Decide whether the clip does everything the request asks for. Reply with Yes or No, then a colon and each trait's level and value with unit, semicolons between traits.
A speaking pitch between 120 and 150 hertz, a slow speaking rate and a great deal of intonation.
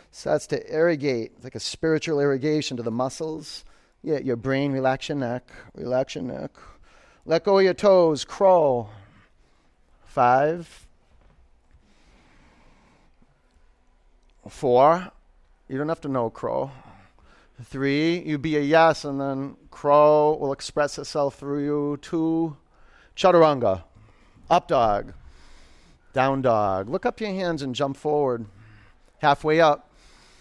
Yes: low, 135 Hz; slow, 125 wpm; wide, 7.2 semitones